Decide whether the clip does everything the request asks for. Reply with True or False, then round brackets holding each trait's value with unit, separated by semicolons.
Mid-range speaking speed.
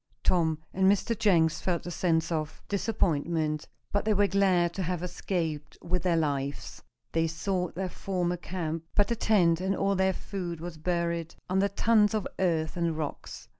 True (170 wpm)